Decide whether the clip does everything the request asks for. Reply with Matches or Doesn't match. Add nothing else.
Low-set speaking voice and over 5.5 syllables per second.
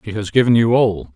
Matches